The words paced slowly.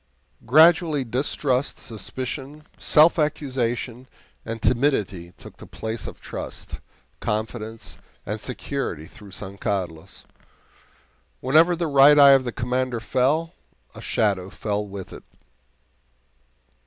Yes: slow, 110 wpm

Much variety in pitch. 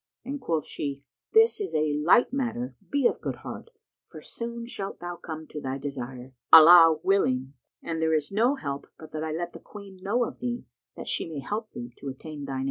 Yes: wide, 7.4 semitones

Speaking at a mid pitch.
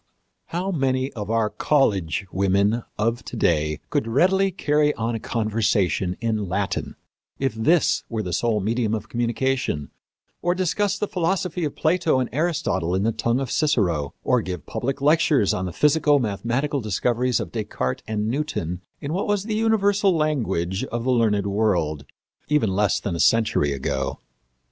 No: low, 115 Hz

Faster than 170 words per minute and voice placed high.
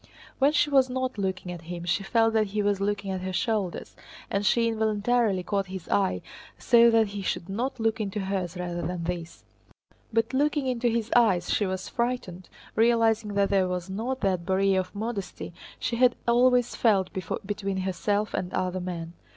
Yes: average, 180 wpm; high, 205 Hz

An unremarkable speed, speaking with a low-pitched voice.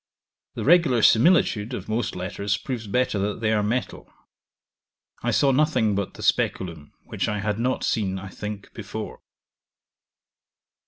Yes: average, 145 wpm; low, 105 Hz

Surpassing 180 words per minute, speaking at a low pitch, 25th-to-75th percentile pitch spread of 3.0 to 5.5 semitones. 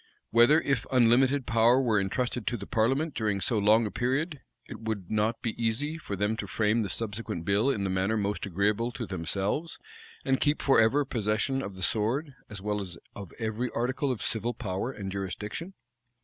Yes: average, 190 wpm; low, 110 Hz; average, 3.9 semitones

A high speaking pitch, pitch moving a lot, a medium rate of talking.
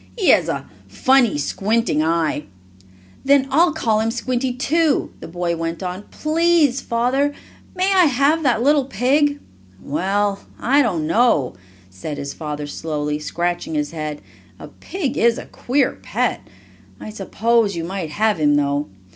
Yes: high, 220 Hz; wide, 9.0 semitones; average, 150 wpm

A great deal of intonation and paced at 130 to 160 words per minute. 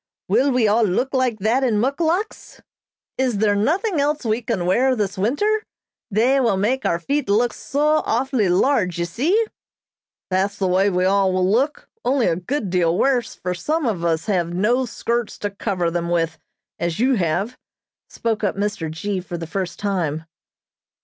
No: wide, 6.2 semitones; average, 175 wpm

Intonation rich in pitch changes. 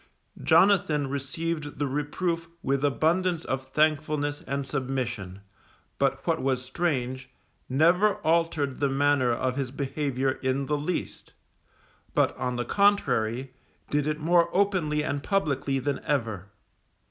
No: average, 3.3 semitones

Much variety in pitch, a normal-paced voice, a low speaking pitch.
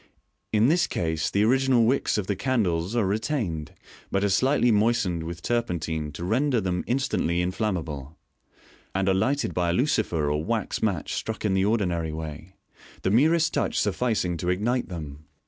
Yes: wide, 5.7 semitones; average, 165 wpm; very low, 95 Hz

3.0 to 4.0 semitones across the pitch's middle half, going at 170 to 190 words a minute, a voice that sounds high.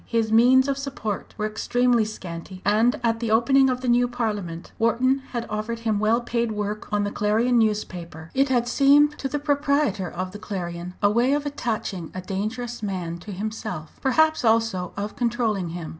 Yes: average, 3.4 semitones; average, 185 wpm; high, 225 Hz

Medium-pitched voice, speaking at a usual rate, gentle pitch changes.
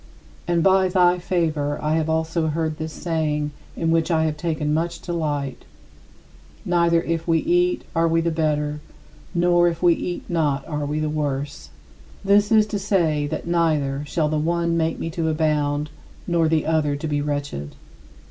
Yes: medium, 160 Hz; average, 175 wpm; narrow, 2.3 semitones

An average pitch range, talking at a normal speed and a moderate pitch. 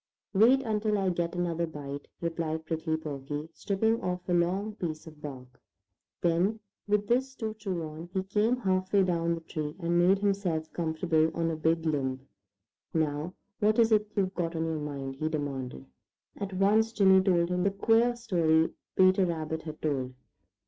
Yes: average, 4.0 semitones; average, 175 wpm; medium, 170 Hz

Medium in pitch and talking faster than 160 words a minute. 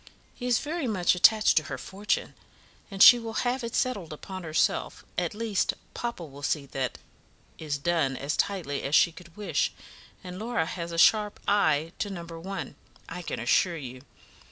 Yes: medium, 180 Hz; average, 180 wpm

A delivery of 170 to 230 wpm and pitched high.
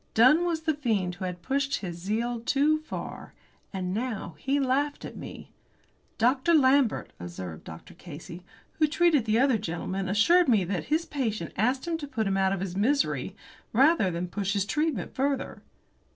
Yes: average, 175 wpm; high, 230 Hz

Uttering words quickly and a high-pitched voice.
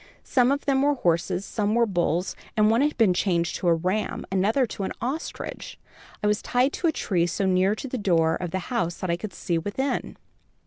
Yes: fast, 220 wpm; high, 200 Hz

